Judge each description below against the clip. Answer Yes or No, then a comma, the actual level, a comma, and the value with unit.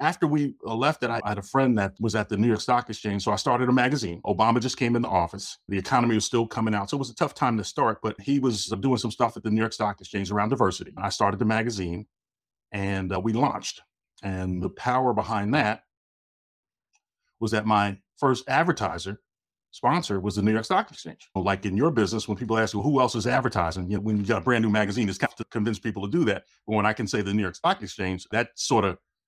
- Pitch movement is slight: No, average, 3.2 semitones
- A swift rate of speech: Yes, fast, 250 wpm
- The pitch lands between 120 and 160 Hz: No, low, 110 Hz